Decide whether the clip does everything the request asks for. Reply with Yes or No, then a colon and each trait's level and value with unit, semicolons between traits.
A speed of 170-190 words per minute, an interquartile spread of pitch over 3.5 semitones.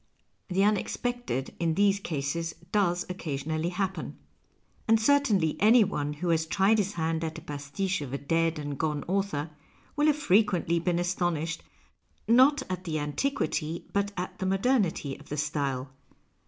No: average, 155 wpm; average, 4.7 semitones